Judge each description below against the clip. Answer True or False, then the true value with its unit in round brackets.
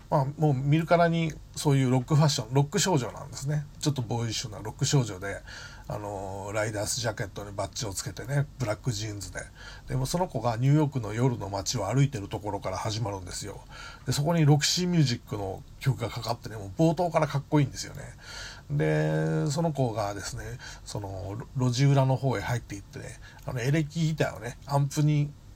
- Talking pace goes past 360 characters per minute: True (455 characters per minute)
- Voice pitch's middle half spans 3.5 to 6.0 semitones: True (5.1 semitones)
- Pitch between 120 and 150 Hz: True (130 Hz)